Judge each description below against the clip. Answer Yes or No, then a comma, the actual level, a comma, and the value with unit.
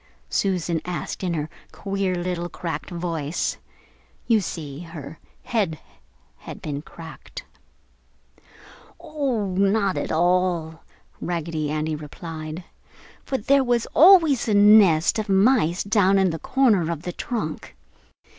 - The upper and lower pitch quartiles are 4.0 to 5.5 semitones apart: Yes, average, 4.5 semitones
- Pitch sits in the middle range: Yes, medium, 180 Hz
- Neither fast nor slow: No, slow, 120 wpm